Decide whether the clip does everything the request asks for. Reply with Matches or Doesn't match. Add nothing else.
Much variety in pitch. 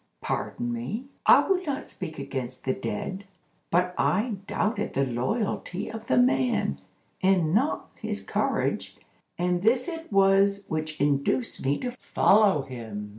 Matches